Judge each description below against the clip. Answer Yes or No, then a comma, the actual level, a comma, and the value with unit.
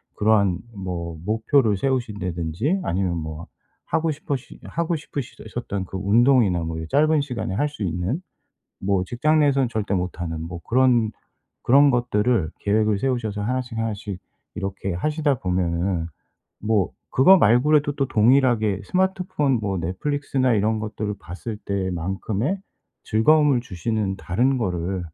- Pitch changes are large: Yes, wide, 6.1 semitones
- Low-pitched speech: Yes, low, 110 Hz